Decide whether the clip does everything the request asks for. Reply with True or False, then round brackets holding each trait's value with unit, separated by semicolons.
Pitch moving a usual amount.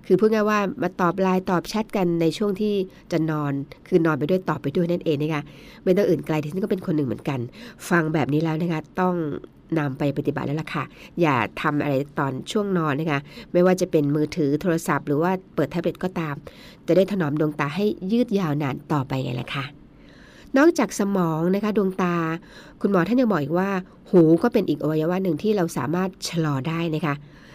True (3.8 semitones)